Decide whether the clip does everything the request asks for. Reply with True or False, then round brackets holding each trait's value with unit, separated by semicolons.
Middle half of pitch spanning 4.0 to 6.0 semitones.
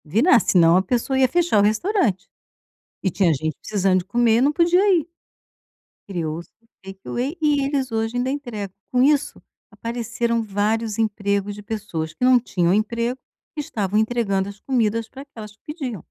True (4.5 semitones)